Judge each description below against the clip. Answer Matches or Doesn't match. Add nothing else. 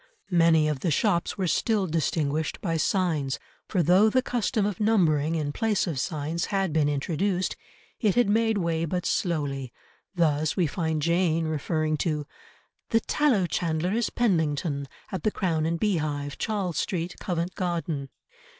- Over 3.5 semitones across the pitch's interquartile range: Matches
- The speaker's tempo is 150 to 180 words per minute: Matches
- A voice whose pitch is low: Doesn't match